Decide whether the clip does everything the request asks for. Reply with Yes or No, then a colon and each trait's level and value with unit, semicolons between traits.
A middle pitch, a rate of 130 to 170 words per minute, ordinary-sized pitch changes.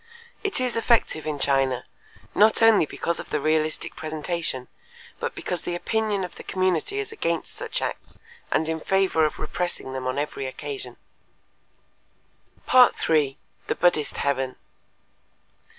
No: medium, 160 Hz; slow, 135 wpm; wide, 5.9 semitones